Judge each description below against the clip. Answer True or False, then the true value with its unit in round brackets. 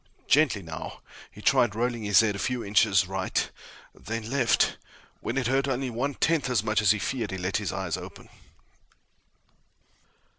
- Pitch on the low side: True (115 Hz)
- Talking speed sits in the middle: True (170 wpm)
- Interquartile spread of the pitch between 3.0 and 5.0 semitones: True (4.0 semitones)